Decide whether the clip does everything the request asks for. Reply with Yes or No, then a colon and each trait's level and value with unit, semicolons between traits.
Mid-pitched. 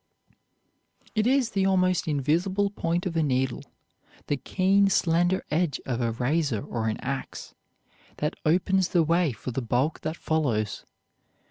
Yes: medium, 160 Hz